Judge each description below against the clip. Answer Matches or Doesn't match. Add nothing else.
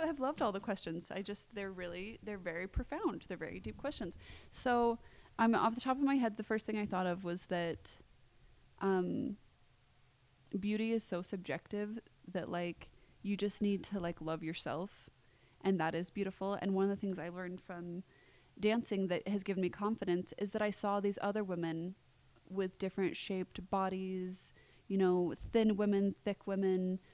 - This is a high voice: Matches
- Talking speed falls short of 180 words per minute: Doesn't match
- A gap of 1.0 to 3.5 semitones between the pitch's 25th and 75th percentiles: Matches